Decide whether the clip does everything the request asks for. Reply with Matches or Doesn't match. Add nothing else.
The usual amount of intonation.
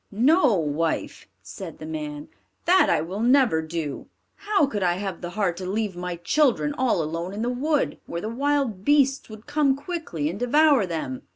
Doesn't match